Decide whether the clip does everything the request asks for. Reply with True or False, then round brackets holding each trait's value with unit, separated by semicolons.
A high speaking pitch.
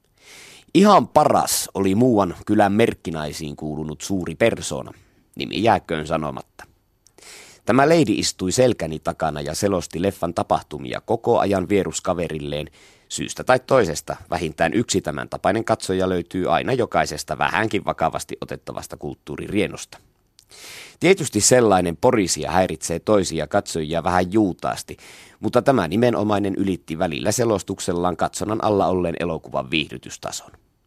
False (90 Hz)